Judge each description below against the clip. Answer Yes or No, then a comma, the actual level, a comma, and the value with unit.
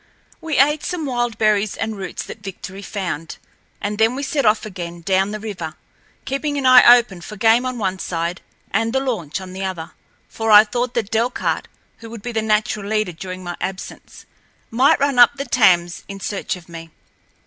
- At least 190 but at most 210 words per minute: Yes, average, 195 wpm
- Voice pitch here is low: No, high, 215 Hz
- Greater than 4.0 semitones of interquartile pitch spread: Yes, average, 4.4 semitones